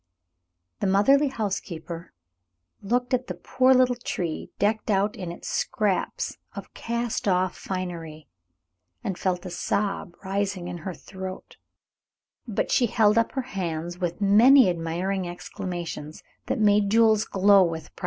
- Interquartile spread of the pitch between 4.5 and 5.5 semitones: No, average, 3.7 semitones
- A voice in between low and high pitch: No, high, 195 Hz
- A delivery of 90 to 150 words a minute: Yes, average, 140 wpm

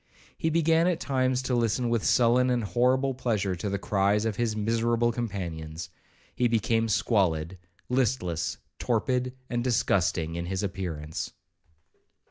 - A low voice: Yes, low, 115 Hz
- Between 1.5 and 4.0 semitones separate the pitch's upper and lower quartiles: No, average, 4.6 semitones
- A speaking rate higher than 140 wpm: No, slow, 135 wpm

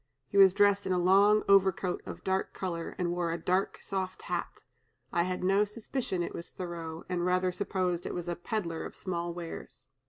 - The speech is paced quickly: No, average, 195 wpm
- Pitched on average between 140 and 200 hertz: Yes, medium, 185 Hz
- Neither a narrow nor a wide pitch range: No, narrow, 2.1 semitones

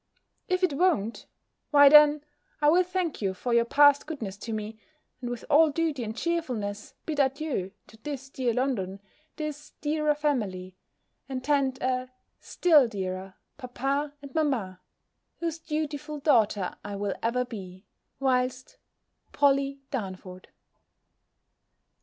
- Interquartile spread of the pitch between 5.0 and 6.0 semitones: Yes, wide, 5.5 semitones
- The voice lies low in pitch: No, very high, 265 Hz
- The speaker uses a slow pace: Yes, slow, 130 wpm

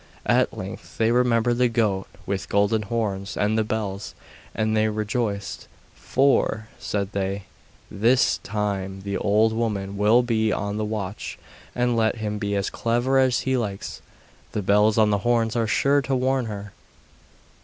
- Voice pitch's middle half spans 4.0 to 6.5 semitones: No, narrow, 2.5 semitones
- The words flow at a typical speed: Yes, average, 160 wpm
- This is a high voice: No, low, 110 Hz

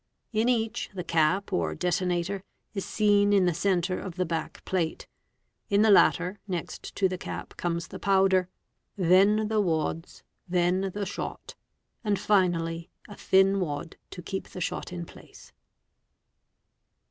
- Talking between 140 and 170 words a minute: Yes, average, 145 wpm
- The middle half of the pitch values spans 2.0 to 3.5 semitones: Yes, narrow, 2.5 semitones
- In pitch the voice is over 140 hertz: Yes, medium, 185 Hz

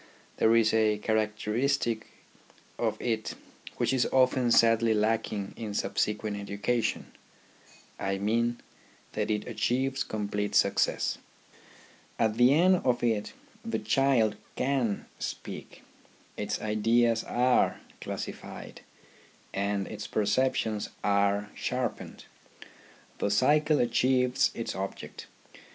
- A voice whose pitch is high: No, low, 115 Hz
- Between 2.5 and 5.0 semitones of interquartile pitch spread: Yes, average, 3.0 semitones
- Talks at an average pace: No, slow, 105 wpm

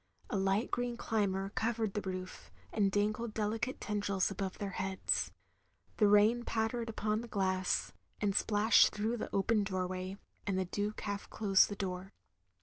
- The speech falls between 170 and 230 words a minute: No, average, 155 wpm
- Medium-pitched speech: No, high, 205 Hz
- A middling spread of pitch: No, narrow, 2.3 semitones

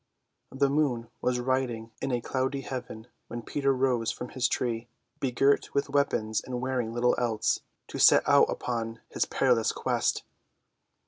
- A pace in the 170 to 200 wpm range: No, average, 150 wpm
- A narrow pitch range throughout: Yes, narrow, 2.3 semitones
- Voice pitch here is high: No, low, 125 Hz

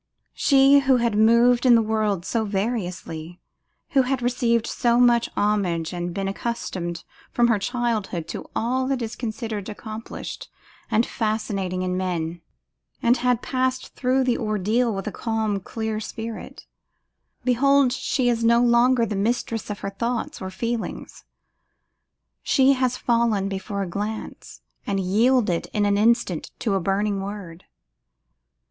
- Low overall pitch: No, high, 220 Hz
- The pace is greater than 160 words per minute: No, average, 145 wpm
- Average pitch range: Yes, average, 3.5 semitones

